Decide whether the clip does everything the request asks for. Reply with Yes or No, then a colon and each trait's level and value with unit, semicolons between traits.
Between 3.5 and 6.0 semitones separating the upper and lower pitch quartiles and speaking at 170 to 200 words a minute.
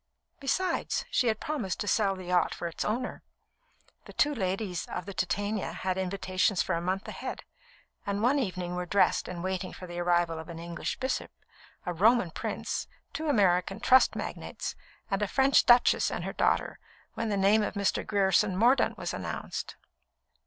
Yes: average, 3.8 semitones; average, 175 wpm